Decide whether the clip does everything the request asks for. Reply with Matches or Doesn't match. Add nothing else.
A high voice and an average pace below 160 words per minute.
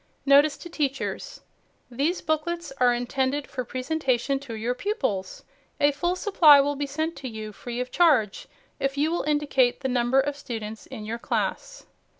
Doesn't match